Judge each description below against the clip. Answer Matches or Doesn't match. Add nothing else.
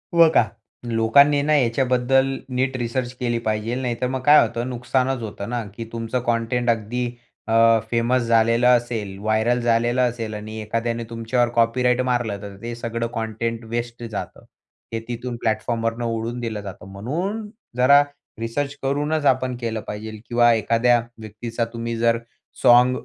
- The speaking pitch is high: Doesn't match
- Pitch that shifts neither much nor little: Doesn't match